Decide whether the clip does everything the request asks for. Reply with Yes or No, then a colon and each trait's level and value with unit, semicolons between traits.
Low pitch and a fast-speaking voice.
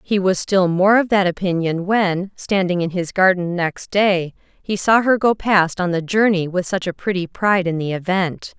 No: medium, 185 Hz; fast, 210 wpm